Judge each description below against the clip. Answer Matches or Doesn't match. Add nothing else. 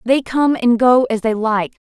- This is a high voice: Matches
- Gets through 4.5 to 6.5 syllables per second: Doesn't match